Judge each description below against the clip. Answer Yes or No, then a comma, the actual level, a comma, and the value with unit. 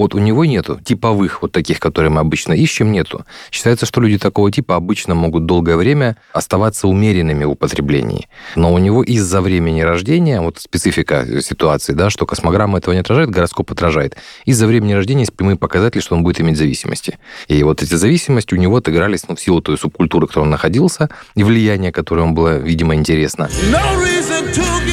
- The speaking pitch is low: Yes, very low, 95 Hz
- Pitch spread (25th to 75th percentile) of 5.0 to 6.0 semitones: Yes, wide, 5.4 semitones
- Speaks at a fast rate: Yes, fast, 185 wpm